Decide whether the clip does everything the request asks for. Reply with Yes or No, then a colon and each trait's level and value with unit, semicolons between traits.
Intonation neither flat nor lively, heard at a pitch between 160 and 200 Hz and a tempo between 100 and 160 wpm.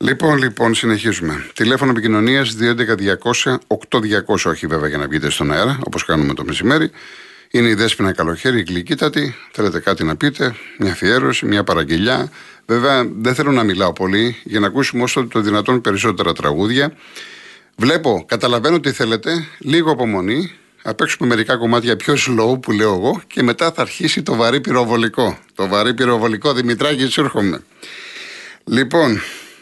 No: average, 4.4 semitones; low, 120 Hz; average, 150 wpm